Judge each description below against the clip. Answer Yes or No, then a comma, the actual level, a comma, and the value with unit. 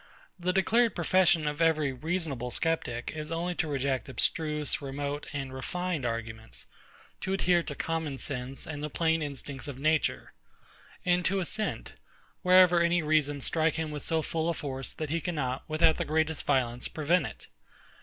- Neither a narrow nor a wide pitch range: Yes, average, 3.6 semitones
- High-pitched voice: No, medium, 155 Hz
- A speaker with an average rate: Yes, average, 165 wpm